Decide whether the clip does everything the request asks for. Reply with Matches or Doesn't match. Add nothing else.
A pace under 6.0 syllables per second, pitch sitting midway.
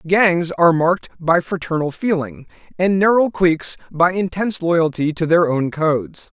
Matches